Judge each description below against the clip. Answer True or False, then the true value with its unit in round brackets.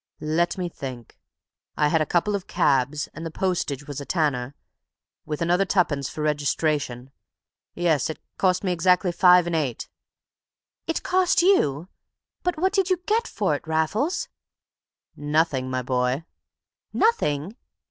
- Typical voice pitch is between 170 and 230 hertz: False (160 Hz)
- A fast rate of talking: False (145 wpm)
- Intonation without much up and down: False (4.6 semitones)